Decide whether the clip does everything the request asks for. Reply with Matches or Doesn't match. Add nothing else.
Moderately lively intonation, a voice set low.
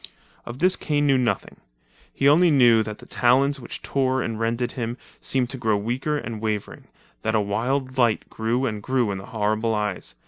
Matches